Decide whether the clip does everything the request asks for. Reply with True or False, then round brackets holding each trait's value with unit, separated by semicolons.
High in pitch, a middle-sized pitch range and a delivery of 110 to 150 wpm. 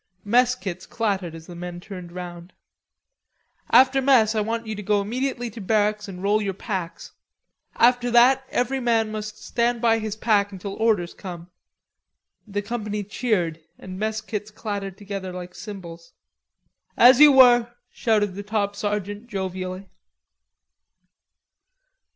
True (210 Hz; 3.5 semitones; 140 wpm)